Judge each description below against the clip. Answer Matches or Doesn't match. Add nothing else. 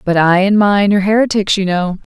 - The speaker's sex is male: Doesn't match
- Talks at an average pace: Doesn't match